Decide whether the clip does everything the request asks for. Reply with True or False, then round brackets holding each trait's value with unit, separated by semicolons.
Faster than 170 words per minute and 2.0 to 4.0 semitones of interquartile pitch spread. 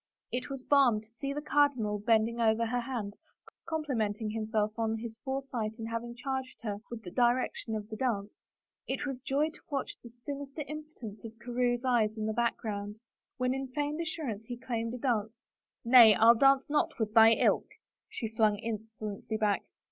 True (180 wpm; 3.3 semitones)